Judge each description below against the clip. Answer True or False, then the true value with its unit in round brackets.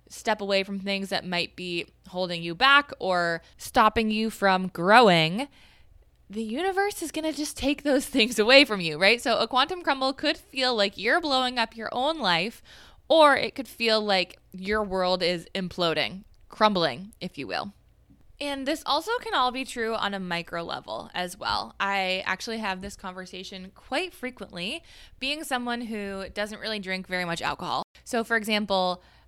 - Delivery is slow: False (175 wpm)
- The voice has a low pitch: False (215 Hz)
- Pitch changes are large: True (5.7 semitones)